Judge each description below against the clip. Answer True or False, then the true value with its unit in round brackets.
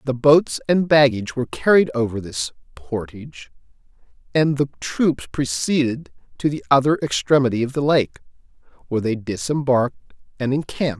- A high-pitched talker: False (130 Hz)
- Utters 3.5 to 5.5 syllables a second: True (5.2 syllables/s)